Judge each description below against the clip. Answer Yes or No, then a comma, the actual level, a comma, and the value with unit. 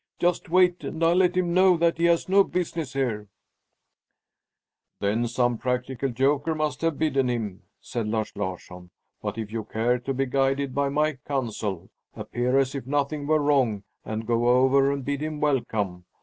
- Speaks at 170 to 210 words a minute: Yes, average, 175 wpm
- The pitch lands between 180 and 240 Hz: No, low, 135 Hz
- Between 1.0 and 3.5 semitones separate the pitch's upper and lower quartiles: No, average, 4.9 semitones